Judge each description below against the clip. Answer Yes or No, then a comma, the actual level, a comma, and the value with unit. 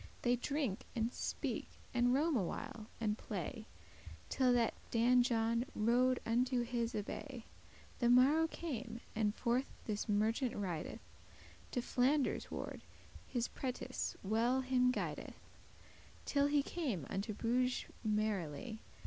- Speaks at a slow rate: Yes, slow, 125 wpm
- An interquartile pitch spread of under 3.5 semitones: Yes, average, 2.7 semitones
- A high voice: Yes, high, 240 Hz